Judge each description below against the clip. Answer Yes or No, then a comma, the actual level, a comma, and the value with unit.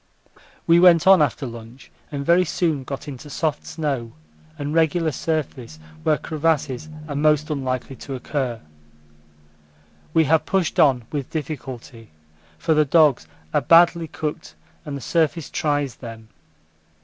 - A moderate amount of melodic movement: Yes, average, 3.4 semitones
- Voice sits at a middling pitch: Yes, medium, 145 Hz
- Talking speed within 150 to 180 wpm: No, slow, 135 wpm